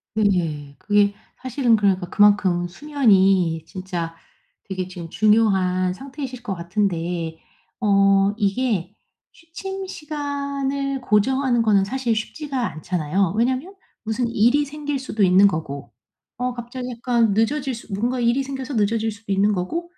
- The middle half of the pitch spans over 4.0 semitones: Yes, wide, 5.6 semitones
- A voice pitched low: No, high, 215 Hz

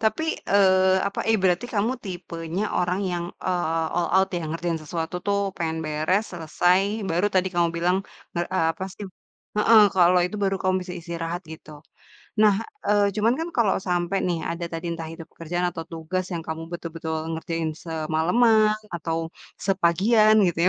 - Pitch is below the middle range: No, medium, 175 Hz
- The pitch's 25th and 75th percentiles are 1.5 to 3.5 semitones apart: Yes, average, 2.9 semitones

